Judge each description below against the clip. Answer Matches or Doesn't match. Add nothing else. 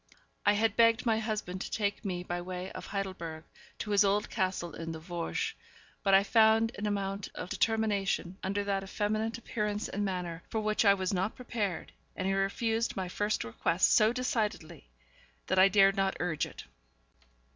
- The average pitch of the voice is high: Matches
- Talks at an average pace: Matches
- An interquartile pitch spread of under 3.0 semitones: Matches